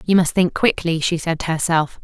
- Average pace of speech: No, fast, 235 wpm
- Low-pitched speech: No, medium, 170 Hz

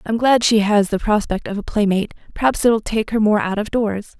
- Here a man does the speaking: No, female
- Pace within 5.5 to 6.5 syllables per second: Yes, 5.8 syllables/s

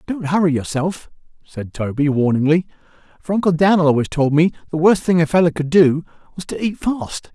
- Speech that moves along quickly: No, average, 190 wpm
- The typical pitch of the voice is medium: Yes, medium, 160 Hz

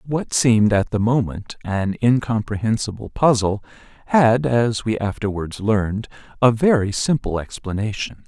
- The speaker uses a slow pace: Yes, slow, 125 wpm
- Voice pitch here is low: Yes, low, 110 Hz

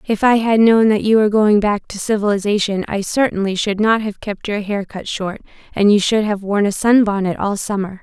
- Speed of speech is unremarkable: No, fast, 215 wpm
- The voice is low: No, high, 205 Hz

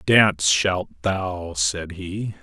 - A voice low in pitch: Yes, very low, 90 Hz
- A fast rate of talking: No, slow, 125 wpm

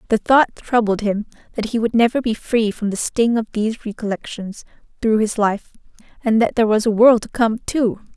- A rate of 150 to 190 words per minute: No, fast, 205 wpm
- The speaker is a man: No, female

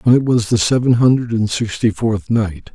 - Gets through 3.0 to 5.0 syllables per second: Yes, 4.9 syllables/s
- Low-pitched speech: Yes, low, 110 Hz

